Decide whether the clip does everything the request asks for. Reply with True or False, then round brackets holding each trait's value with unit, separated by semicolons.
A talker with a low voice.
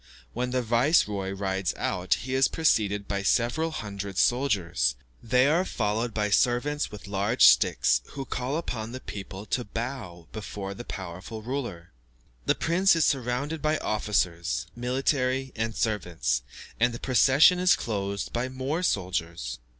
True (115 Hz)